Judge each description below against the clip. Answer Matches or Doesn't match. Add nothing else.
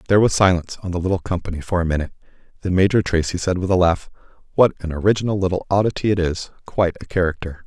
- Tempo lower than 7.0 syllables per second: Doesn't match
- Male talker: Matches